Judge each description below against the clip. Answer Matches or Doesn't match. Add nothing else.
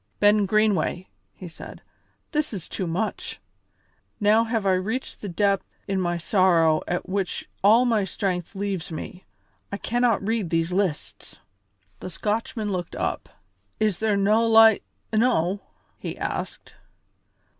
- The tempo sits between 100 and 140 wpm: Matches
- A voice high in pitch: Matches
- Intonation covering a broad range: Doesn't match